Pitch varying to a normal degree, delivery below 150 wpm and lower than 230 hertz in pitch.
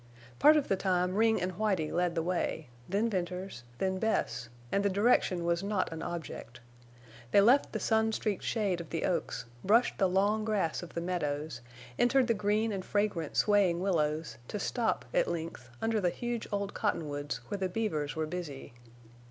No: average, 4.3 semitones; average, 180 wpm; medium, 185 Hz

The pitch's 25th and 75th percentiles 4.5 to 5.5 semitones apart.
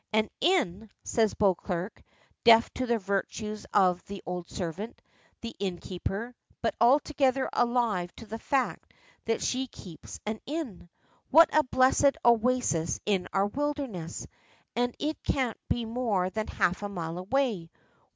Yes: average, 5.1 semitones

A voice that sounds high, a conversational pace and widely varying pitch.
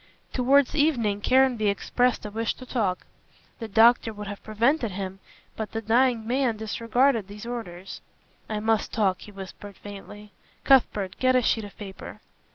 No: high, 220 Hz; average, 160 wpm; average, 3.2 semitones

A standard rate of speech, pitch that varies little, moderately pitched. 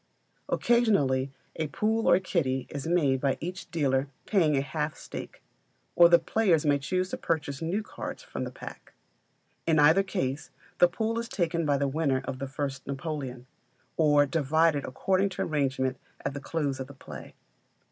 No: average, 165 wpm; average, 4.1 semitones; medium, 150 Hz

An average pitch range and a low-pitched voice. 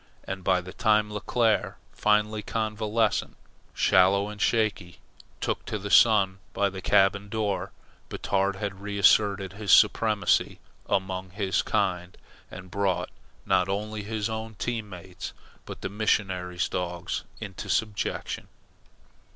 No: narrow, 2.1 semitones; low, 100 Hz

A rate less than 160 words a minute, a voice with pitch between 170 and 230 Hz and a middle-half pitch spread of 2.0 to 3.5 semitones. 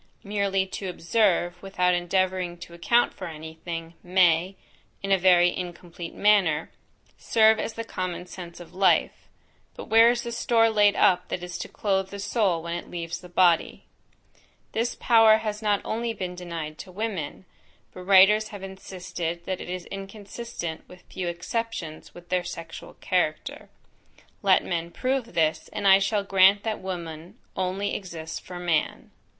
No: average, 165 wpm; medium, 185 Hz; average, 2.9 semitones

